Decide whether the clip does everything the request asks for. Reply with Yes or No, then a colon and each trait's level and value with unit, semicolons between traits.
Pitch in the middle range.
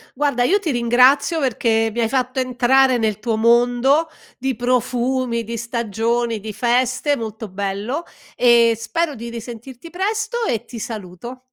No: high, 240 Hz